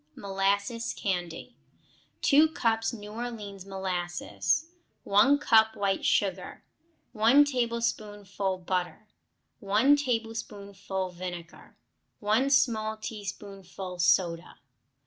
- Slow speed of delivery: Yes, slow, 85 wpm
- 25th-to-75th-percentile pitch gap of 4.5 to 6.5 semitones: No, average, 3.3 semitones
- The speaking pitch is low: No, high, 205 Hz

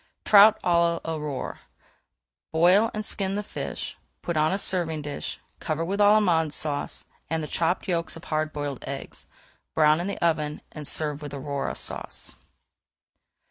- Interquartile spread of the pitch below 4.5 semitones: Yes, average, 3.3 semitones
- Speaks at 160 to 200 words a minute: No, average, 150 wpm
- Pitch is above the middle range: No, medium, 160 Hz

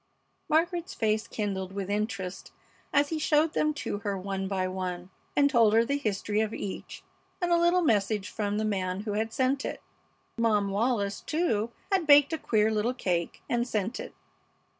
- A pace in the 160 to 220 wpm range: Yes, average, 180 wpm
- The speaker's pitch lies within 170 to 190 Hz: No, high, 215 Hz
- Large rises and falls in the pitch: Yes, wide, 6.0 semitones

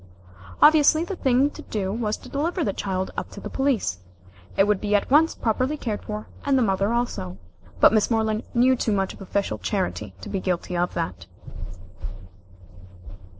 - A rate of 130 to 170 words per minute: No, average, 180 wpm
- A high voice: Yes, high, 215 Hz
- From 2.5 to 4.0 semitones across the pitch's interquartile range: No, wide, 5.5 semitones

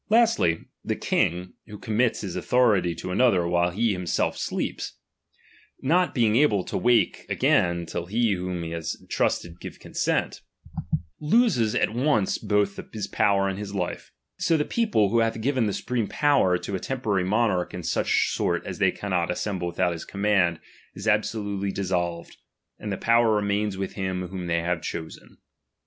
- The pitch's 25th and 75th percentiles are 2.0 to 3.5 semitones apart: No, average, 4.4 semitones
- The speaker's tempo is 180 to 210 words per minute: No, average, 165 wpm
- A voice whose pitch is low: Yes, low, 100 Hz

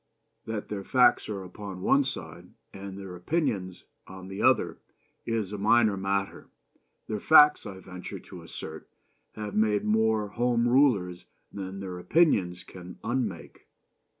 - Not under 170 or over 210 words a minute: No, average, 140 wpm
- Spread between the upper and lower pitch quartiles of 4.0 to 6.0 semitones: No, average, 3.4 semitones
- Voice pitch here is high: No, low, 100 Hz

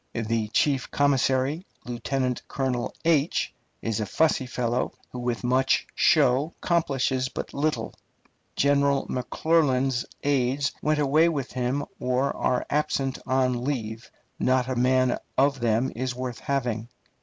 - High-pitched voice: No, low, 130 Hz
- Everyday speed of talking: No, slow, 125 wpm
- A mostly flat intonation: Yes, narrow, 2.3 semitones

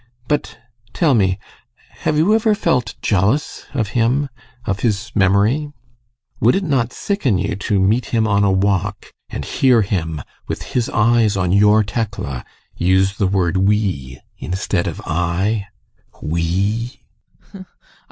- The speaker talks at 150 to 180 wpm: No, slow, 135 wpm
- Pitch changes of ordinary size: Yes, average, 4.0 semitones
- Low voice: Yes, low, 105 Hz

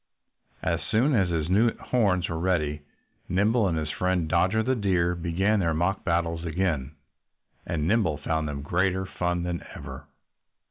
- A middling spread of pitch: Yes, average, 3.0 semitones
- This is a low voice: Yes, very low, 90 Hz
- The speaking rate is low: No, average, 155 wpm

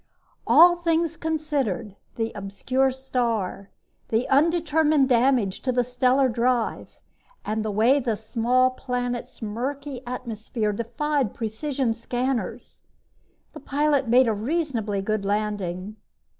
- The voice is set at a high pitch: Yes, high, 245 Hz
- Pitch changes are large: No, average, 4.1 semitones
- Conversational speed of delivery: No, slow, 115 wpm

